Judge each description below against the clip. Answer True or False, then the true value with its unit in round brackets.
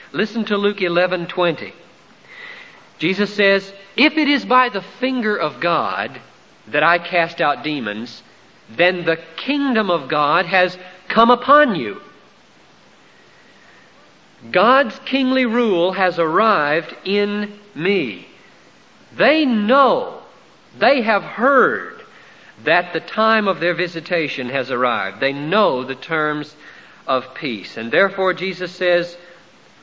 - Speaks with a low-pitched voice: False (185 Hz)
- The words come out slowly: True (120 wpm)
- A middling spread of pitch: True (5.0 semitones)